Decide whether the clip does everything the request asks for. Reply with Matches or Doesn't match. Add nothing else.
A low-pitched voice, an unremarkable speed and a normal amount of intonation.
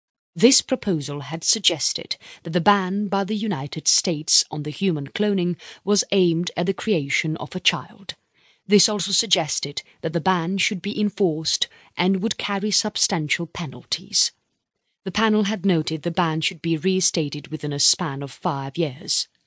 Doesn't match